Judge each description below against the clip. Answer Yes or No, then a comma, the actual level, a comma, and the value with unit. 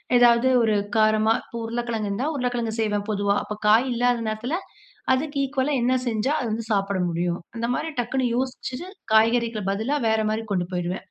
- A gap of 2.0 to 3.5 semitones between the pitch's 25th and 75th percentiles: Yes, average, 2.7 semitones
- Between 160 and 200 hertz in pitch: No, high, 230 Hz